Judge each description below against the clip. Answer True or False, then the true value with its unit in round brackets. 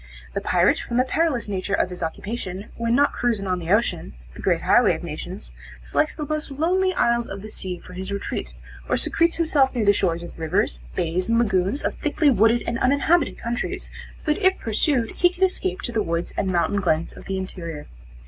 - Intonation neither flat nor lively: False (7.4 semitones)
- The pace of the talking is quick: True (210 wpm)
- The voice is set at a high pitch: True (225 Hz)